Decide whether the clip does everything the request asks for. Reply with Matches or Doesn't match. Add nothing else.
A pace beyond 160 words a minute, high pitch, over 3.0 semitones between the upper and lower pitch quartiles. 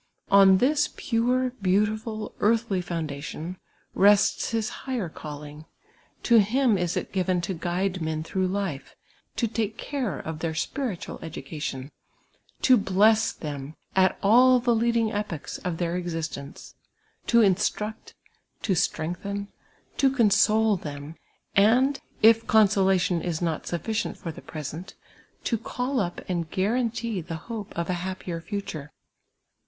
Doesn't match